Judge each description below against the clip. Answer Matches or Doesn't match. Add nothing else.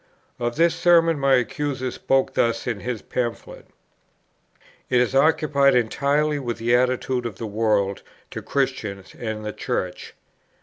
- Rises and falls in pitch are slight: Doesn't match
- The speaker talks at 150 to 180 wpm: Doesn't match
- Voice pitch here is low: Matches